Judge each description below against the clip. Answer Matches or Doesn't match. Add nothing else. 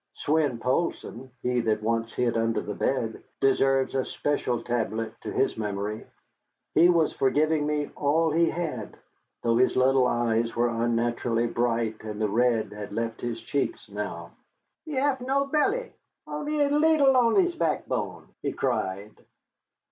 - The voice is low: Matches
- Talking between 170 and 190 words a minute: Doesn't match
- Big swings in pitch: Matches